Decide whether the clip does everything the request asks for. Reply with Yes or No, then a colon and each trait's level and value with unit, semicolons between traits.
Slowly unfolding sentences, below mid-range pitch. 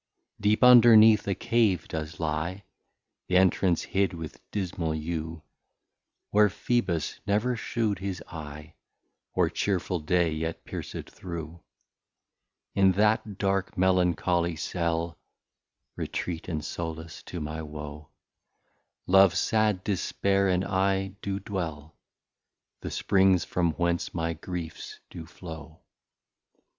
Yes: slow, 110 wpm; very low, 90 Hz